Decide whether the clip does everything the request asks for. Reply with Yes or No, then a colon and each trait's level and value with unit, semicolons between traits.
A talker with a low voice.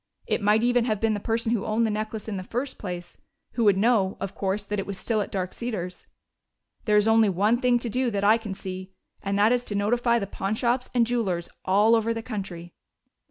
No: high, 215 Hz